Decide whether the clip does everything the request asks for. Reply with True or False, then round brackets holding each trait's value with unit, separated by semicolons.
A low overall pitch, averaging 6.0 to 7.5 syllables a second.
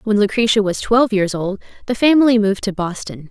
False (210 Hz; 6.1 syllables/s)